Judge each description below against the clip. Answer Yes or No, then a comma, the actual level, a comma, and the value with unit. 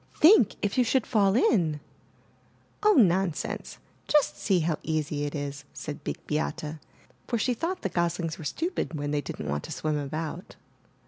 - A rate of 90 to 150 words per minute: No, average, 170 wpm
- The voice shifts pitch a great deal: Yes, wide, 7.0 semitones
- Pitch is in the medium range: Yes, medium, 165 Hz